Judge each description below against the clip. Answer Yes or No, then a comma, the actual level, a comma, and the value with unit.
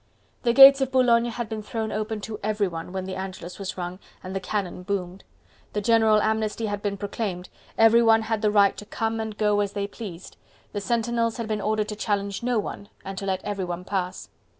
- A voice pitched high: Yes, high, 210 Hz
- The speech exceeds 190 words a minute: Yes, fast, 205 wpm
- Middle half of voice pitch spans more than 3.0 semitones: No, narrow, 2.4 semitones